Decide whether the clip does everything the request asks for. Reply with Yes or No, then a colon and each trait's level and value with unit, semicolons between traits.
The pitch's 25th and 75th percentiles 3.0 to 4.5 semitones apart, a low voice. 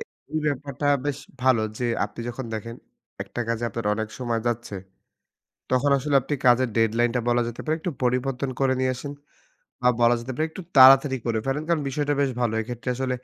No: narrow, 2.5 semitones; low, 125 Hz